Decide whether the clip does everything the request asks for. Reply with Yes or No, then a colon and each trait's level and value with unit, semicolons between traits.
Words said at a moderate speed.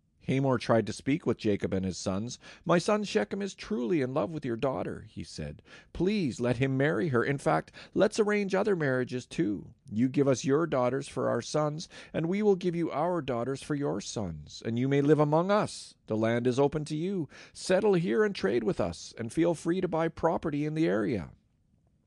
No: fast, 210 wpm